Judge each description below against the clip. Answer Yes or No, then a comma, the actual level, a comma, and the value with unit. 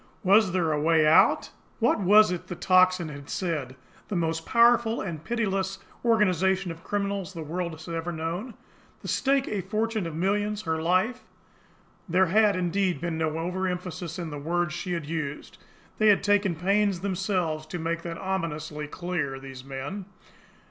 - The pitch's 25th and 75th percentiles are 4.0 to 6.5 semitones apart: No, average, 3.6 semitones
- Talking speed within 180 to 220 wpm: No, average, 165 wpm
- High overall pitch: No, medium, 180 Hz